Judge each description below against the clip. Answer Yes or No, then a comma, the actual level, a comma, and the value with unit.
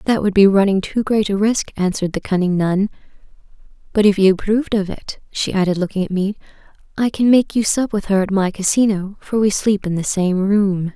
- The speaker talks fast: Yes, fast, 220 wpm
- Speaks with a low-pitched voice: No, high, 200 Hz